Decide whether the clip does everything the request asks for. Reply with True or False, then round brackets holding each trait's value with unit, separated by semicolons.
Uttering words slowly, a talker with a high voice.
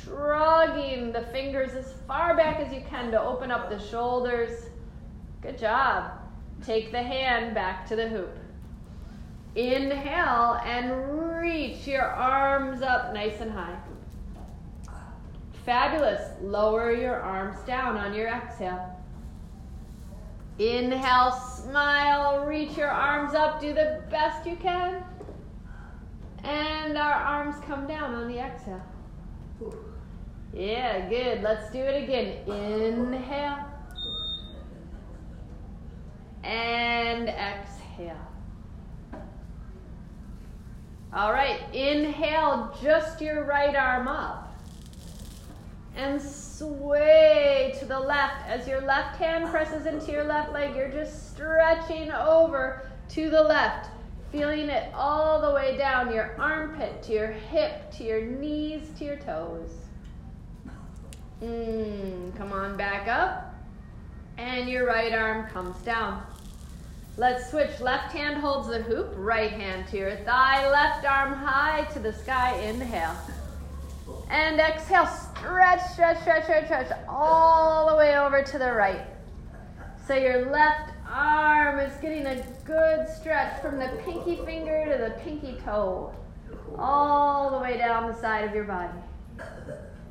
True (125 wpm; 265 Hz)